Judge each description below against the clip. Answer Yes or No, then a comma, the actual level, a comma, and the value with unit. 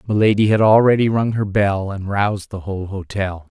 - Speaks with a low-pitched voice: Yes, low, 100 Hz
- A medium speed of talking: Yes, average, 185 wpm